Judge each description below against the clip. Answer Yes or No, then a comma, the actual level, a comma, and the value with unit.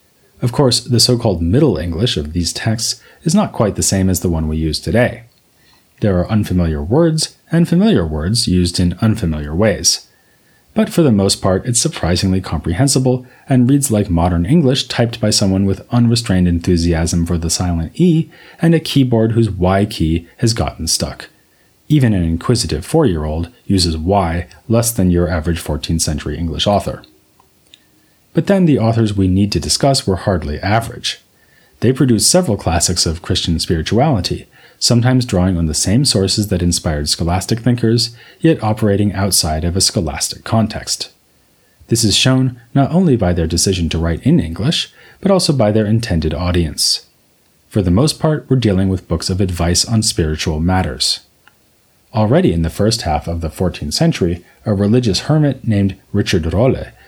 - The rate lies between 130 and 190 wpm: Yes, average, 170 wpm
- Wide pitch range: Yes, wide, 6.0 semitones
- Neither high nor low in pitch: No, low, 100 Hz